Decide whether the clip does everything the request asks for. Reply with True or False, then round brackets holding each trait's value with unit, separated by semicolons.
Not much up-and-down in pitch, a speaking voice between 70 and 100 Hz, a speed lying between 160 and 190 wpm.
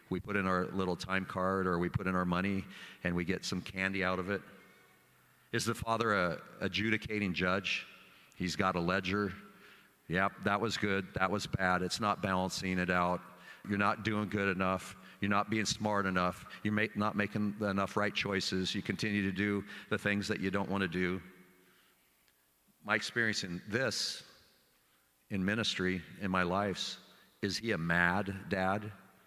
True (2.0 semitones; 95 Hz; 175 wpm)